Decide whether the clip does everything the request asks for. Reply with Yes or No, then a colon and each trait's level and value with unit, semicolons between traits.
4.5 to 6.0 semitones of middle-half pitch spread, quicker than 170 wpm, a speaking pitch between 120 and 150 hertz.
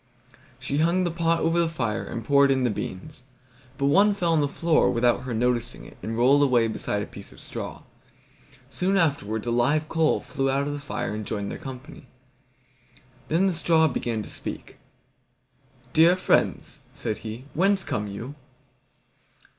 Yes: wide, 5.6 semitones; average, 180 wpm; medium, 140 Hz